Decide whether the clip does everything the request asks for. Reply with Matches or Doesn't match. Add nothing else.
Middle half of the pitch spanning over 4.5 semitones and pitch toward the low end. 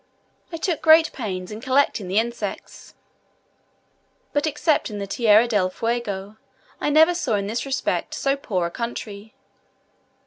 Doesn't match